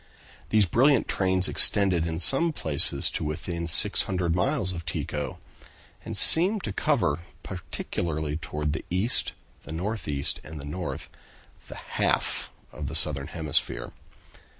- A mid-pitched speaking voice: No, very low, 85 Hz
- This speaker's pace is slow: Yes, slow, 130 wpm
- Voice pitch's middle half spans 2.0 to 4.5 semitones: No, average, 4.9 semitones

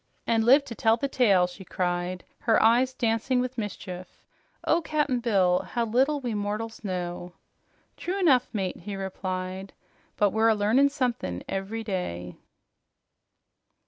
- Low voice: No, high, 220 Hz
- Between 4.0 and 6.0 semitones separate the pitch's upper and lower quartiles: Yes, average, 5.0 semitones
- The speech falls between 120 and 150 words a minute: Yes, average, 145 wpm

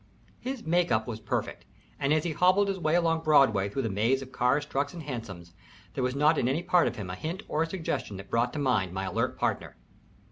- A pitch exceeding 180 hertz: No, medium, 140 Hz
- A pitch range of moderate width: No, wide, 6.6 semitones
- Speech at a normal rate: No, fast, 240 wpm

